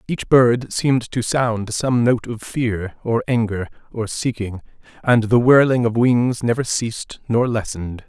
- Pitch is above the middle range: No, low, 115 Hz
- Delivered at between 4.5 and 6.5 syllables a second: No, 4.3 syllables/s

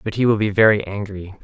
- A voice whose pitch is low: Yes, low, 105 Hz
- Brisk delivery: Yes, fast, 250 wpm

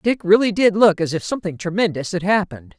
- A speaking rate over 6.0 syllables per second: Yes, 6.2 syllables/s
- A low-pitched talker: No, high, 190 Hz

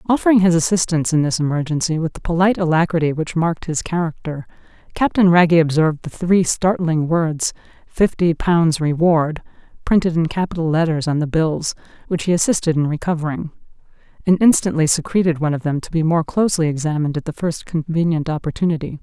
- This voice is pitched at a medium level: Yes, medium, 165 Hz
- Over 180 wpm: No, average, 165 wpm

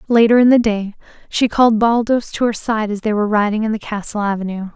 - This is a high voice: Yes, high, 215 Hz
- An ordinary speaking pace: No, fast, 225 wpm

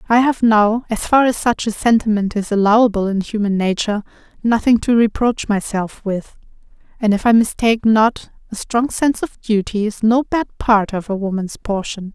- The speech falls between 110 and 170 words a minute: No, average, 185 wpm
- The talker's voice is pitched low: No, high, 220 Hz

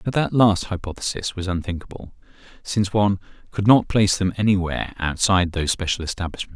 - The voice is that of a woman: No, male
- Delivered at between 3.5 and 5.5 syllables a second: No, 6.3 syllables/s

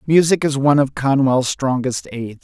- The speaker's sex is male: Yes, male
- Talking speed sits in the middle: Yes, average, 175 wpm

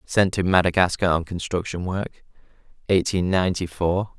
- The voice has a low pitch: Yes, very low, 90 Hz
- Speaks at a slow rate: Yes, slow, 130 wpm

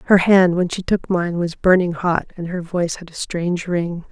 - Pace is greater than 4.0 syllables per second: Yes, 5.0 syllables/s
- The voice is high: No, medium, 175 Hz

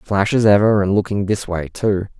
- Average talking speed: No, fast, 220 wpm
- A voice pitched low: Yes, low, 100 Hz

